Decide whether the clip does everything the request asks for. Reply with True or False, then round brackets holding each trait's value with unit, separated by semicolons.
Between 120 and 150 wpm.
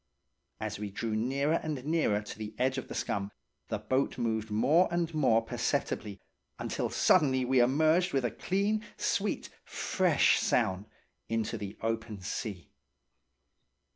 True (140 wpm)